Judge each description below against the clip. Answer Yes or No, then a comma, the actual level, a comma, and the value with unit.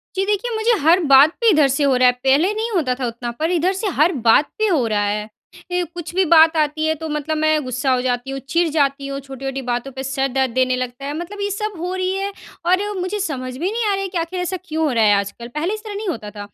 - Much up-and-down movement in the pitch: Yes, wide, 6.0 semitones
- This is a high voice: Yes, very high, 305 Hz